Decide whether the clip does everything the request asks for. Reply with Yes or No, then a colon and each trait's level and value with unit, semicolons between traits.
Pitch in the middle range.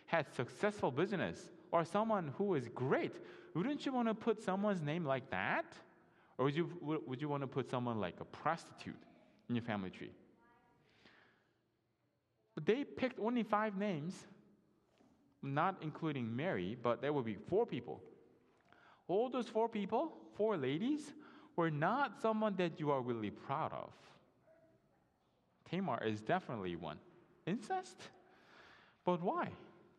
Yes: medium, 170 Hz